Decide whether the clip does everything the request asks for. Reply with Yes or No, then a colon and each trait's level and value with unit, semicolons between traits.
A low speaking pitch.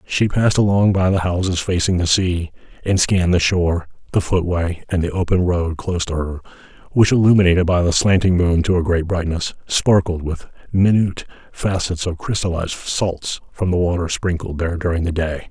Yes: very low, 90 Hz